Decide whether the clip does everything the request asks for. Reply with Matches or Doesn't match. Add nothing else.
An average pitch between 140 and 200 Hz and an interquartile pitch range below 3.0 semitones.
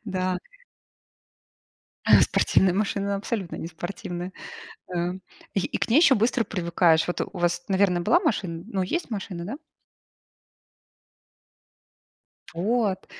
Doesn't match